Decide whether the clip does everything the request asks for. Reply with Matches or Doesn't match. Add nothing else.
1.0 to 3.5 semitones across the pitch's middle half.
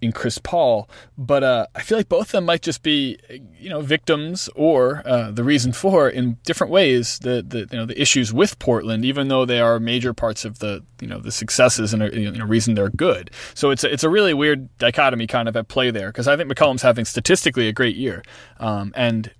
Doesn't match